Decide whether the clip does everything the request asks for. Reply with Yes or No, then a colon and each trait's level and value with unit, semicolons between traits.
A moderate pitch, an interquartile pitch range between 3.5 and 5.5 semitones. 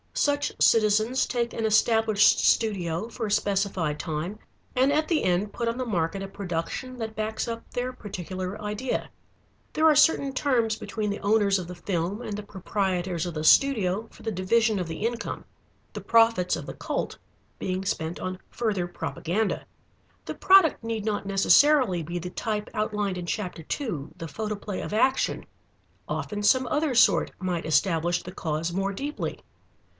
No: high, 205 Hz; average, 4.2 semitones